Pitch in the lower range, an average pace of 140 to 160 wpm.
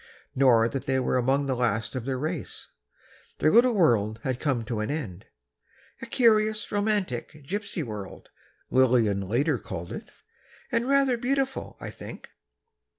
Yes: low, 130 Hz; average, 145 wpm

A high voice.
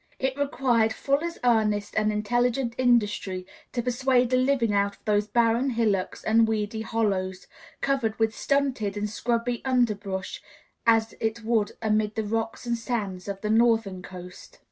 Yes: high, 225 Hz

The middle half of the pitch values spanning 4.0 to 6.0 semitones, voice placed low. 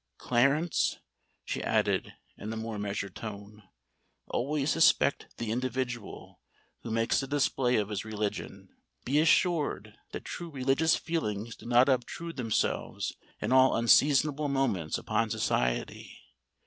Yes: average, 4.7 semitones; low, 125 Hz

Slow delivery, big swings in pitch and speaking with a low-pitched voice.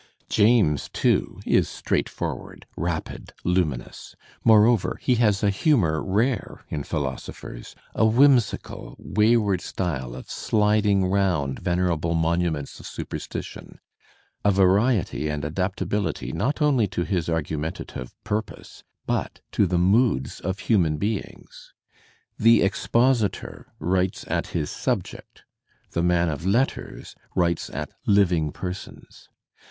No: slow, 115 wpm; average, 4.6 semitones; very low, 95 Hz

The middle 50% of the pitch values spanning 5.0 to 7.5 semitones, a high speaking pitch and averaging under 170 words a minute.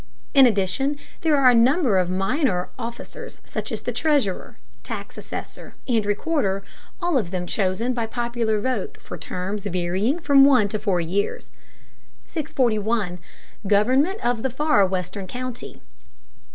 Yes: wide, 5.5 semitones; high, 225 Hz; average, 140 wpm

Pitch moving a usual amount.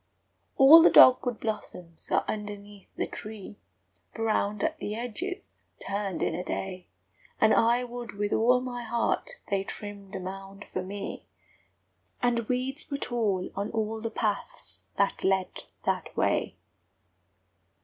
Yes: average, 3.5 semitones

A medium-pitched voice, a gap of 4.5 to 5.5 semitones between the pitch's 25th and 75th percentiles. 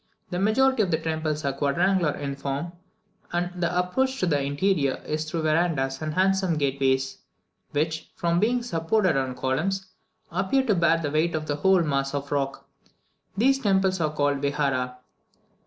Yes: medium, 160 Hz; average, 4.9 semitones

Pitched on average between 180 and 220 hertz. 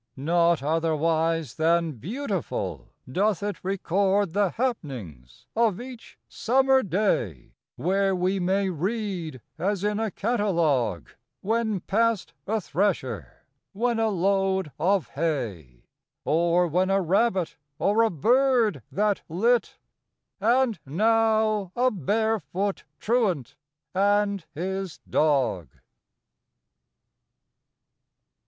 Yes: high, 190 Hz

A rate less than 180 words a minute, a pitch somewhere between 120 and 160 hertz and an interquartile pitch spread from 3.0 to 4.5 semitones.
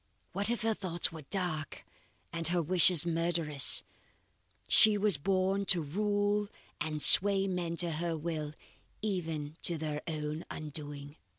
No: slow, 135 wpm; medium, 170 Hz; average, 3.9 semitones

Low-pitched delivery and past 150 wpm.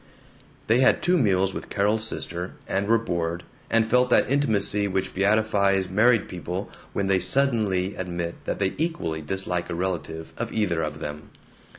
Yes: very low, 95 Hz; average, 165 wpm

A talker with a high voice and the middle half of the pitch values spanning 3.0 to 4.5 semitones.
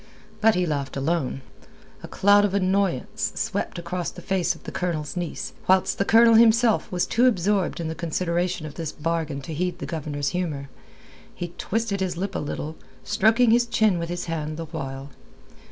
No: medium, 175 Hz; average, 4.0 semitones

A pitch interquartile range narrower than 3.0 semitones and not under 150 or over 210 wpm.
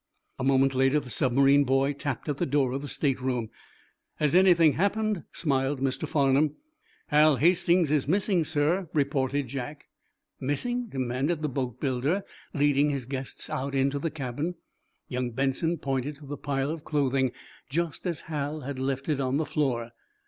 Yes: narrow, 2.6 semitones; average, 165 wpm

